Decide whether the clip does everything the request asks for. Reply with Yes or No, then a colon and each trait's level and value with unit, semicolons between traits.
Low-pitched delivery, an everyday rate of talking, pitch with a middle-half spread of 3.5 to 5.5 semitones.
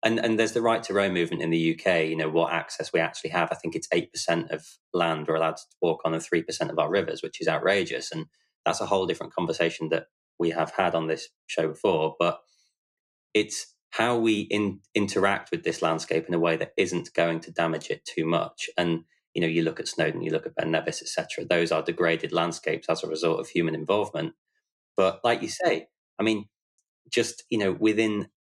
No: very low, 85 Hz; fast, 225 wpm; average, 4.5 semitones